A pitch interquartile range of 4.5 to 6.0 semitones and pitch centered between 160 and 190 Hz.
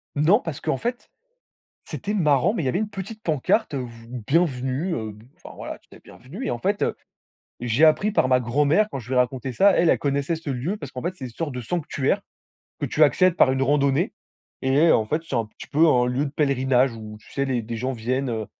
No: average, 4.8 semitones; low, 135 Hz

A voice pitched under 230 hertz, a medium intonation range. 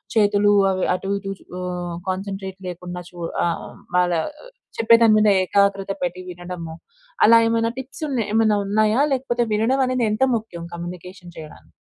Yes: high, 195 Hz; average, 4.0 semitones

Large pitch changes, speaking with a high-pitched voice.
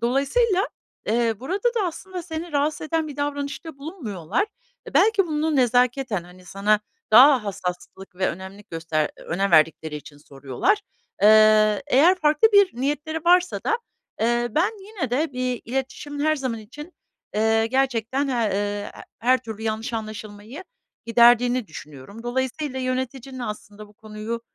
Yes: wide, 5.9 semitones; high, 245 Hz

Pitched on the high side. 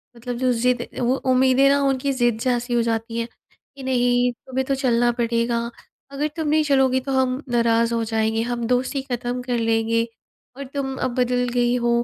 Yes: high, 245 Hz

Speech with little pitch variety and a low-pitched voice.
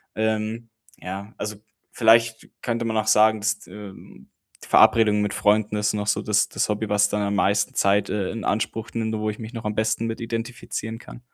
Yes: narrow, 1.4 semitones; low, 110 Hz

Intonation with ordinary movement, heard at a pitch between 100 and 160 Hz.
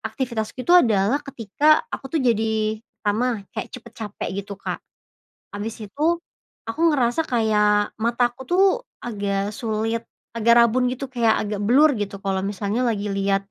No: average, 3.4 semitones; high, 225 Hz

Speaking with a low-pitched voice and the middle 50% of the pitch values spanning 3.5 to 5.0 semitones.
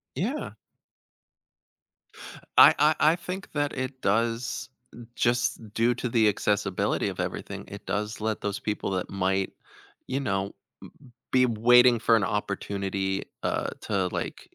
Yes: low, 110 Hz; average, 3.9 semitones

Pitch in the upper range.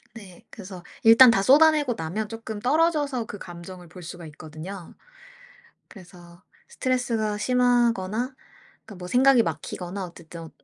Yes: high, 210 Hz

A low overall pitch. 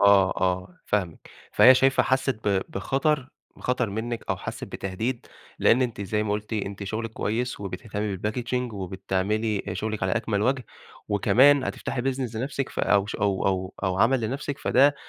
Yes: low, 110 Hz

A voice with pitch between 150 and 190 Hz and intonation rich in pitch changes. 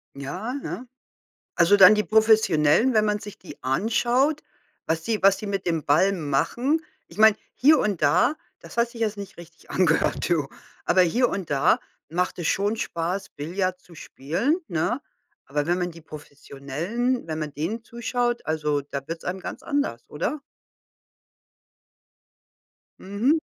Yes: medium, 185 Hz; wide, 6.2 semitones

